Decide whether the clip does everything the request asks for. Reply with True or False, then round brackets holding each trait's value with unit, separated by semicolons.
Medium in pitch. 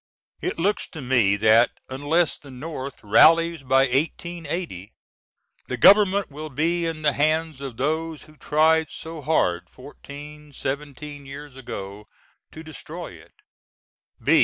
True (150 Hz)